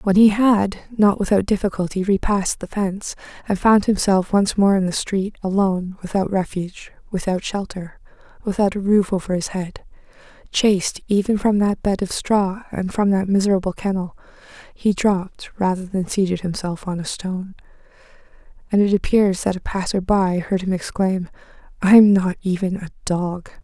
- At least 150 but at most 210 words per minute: Yes, average, 165 wpm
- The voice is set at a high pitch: Yes, high, 195 Hz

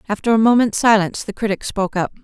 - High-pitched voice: Yes, high, 210 Hz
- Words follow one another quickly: Yes, fast, 215 wpm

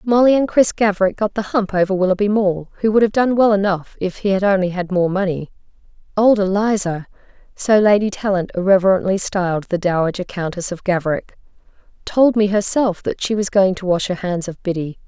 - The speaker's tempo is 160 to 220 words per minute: Yes, average, 180 wpm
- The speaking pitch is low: No, high, 195 Hz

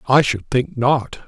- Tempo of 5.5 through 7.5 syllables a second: No, 3.9 syllables/s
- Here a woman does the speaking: No, male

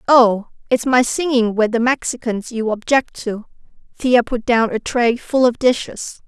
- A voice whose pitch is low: No, high, 235 Hz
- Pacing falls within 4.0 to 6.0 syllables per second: Yes, 4.3 syllables/s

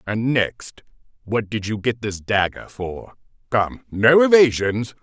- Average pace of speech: Yes, average, 145 wpm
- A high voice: No, low, 115 Hz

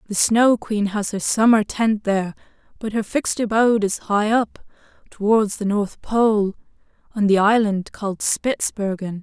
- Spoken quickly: No, average, 155 wpm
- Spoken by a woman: Yes, female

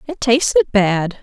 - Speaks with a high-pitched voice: Yes, high, 245 Hz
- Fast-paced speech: No, average, 145 wpm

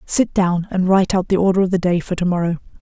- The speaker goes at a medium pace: No, fast, 255 wpm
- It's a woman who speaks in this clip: Yes, female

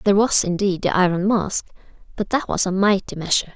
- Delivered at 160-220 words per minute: Yes, fast, 205 wpm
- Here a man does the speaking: No, female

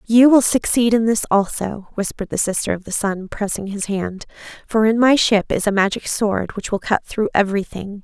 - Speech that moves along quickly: Yes, fast, 210 wpm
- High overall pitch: Yes, high, 205 Hz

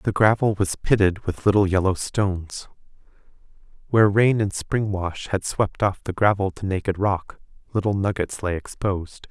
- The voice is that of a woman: No, male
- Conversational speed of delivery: Yes, average, 160 wpm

